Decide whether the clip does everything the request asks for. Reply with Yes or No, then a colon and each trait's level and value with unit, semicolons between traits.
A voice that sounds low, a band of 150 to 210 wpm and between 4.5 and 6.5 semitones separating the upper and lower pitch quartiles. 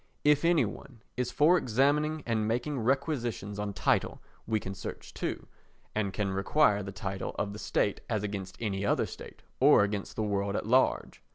Yes: low, 110 Hz; average, 180 wpm; average, 5.0 semitones